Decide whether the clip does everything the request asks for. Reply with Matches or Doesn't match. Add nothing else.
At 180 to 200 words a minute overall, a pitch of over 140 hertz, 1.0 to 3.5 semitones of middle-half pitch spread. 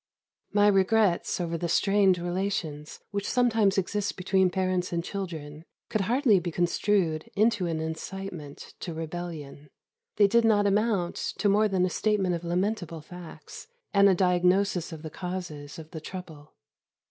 Doesn't match